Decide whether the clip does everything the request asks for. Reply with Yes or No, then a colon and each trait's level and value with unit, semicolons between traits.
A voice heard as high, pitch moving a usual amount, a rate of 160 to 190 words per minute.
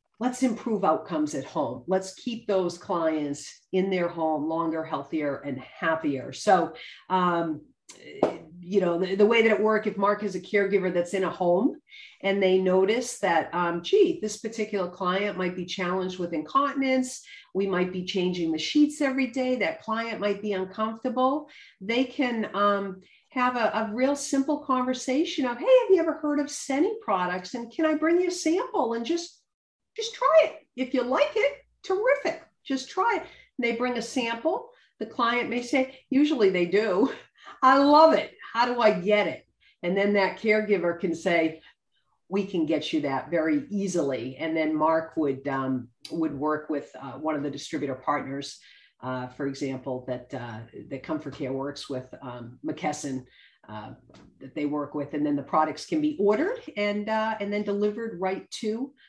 No: high, 205 Hz; wide, 8.2 semitones; average, 180 wpm